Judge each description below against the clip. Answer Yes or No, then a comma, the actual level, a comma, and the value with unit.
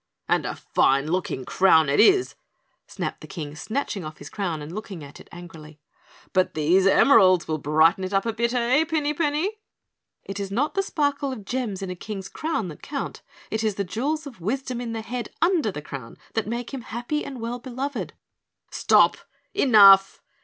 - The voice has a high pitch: Yes, high, 215 Hz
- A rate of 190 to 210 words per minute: Yes, average, 195 wpm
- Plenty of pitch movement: Yes, wide, 6.8 semitones